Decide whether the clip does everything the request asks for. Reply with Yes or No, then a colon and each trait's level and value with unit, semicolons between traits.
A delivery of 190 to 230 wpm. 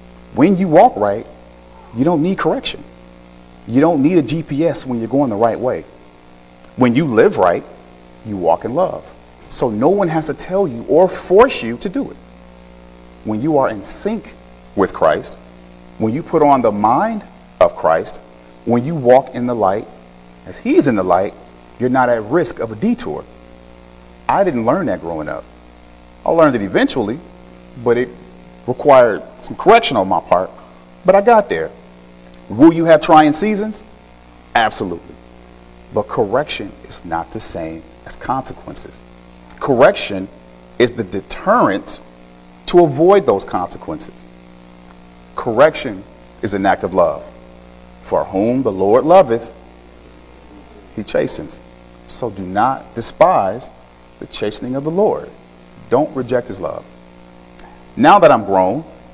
No: average, 150 wpm